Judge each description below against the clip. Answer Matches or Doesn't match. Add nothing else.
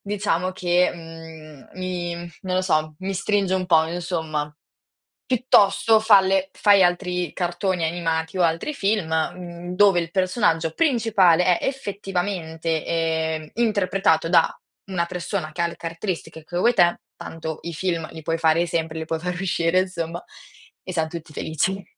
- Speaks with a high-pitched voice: Doesn't match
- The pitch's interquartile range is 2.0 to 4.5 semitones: Matches